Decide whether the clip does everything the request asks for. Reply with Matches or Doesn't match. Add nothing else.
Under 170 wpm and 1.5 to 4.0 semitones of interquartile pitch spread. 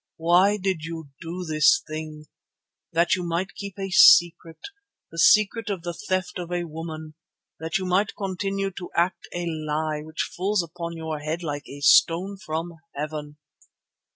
Matches